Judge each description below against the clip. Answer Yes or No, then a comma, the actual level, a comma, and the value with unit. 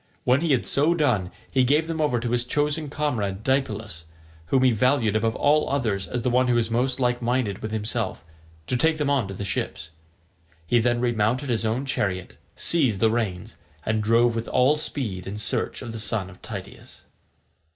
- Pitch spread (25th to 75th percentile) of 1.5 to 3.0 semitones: No, average, 3.7 semitones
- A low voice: Yes, low, 120 Hz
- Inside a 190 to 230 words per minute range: Yes, average, 195 wpm